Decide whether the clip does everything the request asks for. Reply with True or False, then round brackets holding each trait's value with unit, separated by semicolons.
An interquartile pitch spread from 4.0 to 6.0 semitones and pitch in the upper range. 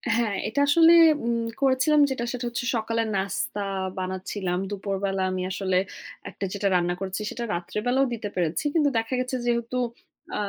True (4.7 semitones; 220 Hz)